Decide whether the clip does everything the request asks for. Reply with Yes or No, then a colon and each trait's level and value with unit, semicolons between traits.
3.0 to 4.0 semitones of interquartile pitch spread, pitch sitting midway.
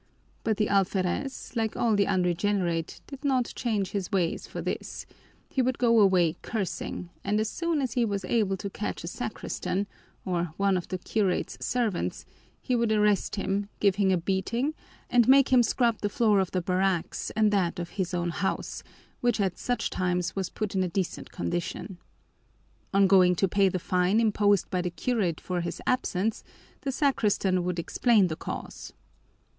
No: average, 3.7 semitones; high, 200 Hz